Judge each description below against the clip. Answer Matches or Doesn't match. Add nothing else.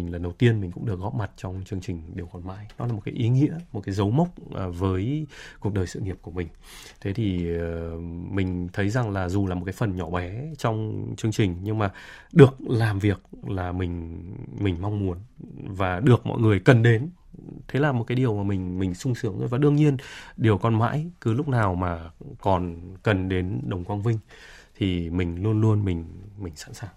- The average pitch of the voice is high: Doesn't match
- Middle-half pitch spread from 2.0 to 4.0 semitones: Doesn't match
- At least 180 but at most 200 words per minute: Doesn't match